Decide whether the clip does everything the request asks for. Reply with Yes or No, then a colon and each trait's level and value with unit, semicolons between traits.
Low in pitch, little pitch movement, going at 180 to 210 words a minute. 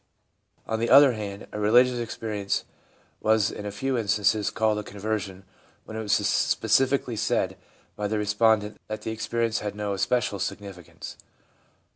No: low, 110 Hz; narrow, 1.8 semitones; average, 150 wpm